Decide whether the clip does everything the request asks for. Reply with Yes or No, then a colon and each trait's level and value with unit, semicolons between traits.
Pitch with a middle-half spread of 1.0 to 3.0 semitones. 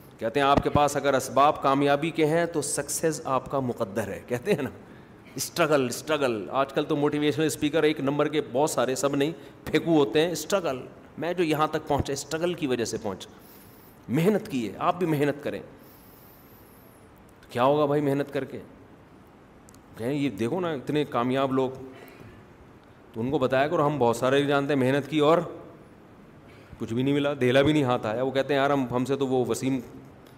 Yes: average, 2.7 semitones